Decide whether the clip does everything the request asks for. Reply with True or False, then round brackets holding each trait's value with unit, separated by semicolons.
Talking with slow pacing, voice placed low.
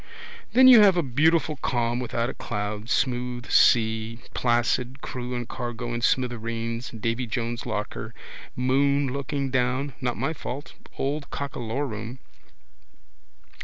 True (130 wpm; 125 Hz)